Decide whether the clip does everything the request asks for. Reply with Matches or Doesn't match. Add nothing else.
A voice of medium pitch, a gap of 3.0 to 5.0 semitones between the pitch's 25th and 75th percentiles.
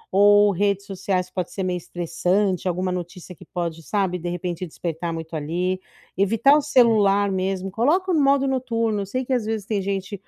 Doesn't match